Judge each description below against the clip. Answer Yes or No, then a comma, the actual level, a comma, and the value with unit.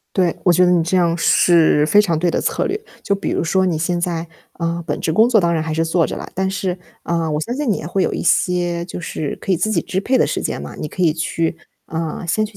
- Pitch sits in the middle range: Yes, medium, 175 Hz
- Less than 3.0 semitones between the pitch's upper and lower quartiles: Yes, narrow, 2.5 semitones